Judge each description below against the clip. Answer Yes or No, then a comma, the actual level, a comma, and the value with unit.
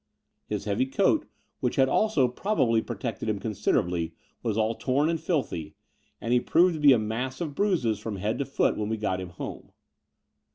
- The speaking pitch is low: Yes, low, 115 Hz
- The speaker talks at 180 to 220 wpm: Yes, average, 190 wpm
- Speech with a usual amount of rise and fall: Yes, average, 4.9 semitones